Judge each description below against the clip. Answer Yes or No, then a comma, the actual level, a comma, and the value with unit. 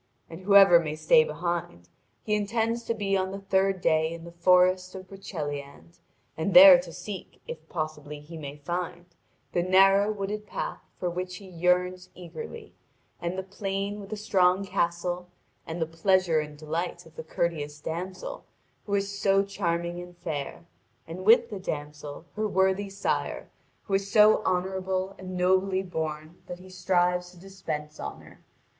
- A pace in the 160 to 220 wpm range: Yes, average, 165 wpm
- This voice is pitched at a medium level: Yes, medium, 180 Hz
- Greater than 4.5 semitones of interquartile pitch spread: No, average, 2.7 semitones